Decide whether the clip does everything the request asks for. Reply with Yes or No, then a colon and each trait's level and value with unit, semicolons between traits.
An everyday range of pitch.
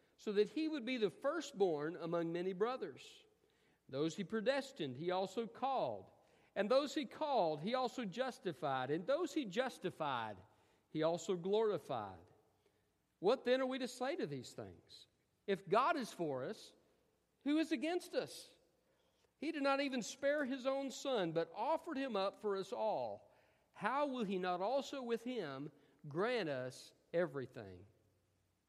No: wide, 8.8 semitones